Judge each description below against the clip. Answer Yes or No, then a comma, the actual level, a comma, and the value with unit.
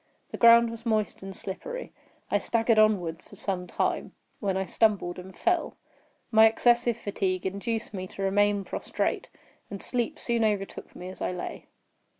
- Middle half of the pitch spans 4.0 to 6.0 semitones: No, average, 3.4 semitones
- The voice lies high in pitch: Yes, high, 205 Hz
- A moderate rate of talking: Yes, average, 160 wpm